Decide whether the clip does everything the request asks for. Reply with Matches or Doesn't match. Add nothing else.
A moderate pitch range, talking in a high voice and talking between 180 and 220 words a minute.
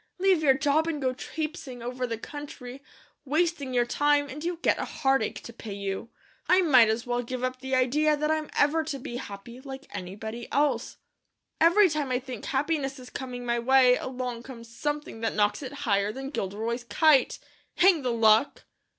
Matches